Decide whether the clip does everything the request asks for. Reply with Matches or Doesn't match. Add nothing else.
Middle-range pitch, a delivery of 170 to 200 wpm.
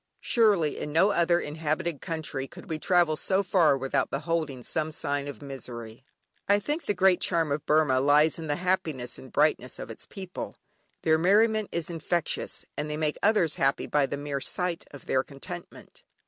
Matches